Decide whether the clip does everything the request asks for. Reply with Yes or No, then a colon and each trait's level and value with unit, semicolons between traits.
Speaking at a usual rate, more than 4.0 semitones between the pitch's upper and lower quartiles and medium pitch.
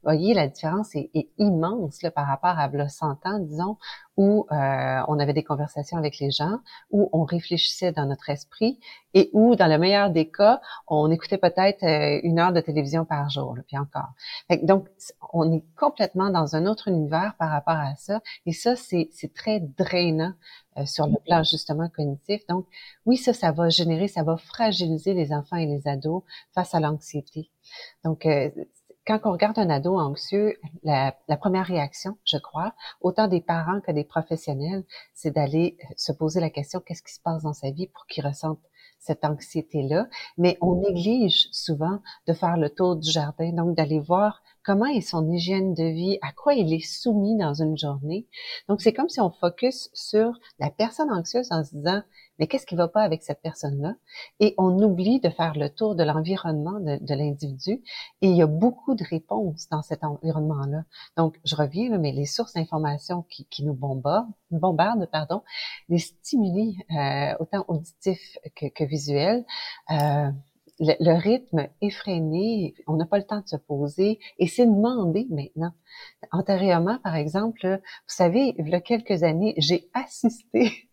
Yes: average, 185 wpm; average, 4.8 semitones; medium, 170 Hz